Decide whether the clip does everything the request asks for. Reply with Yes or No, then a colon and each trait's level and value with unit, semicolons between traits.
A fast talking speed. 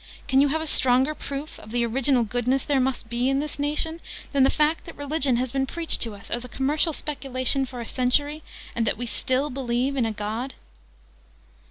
Yes: fast, 210 wpm